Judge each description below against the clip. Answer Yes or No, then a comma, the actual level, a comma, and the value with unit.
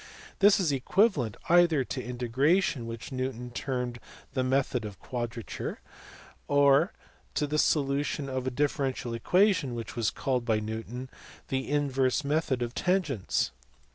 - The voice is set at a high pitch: No, low, 130 Hz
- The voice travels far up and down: No, average, 3.2 semitones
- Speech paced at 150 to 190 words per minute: No, slow, 135 wpm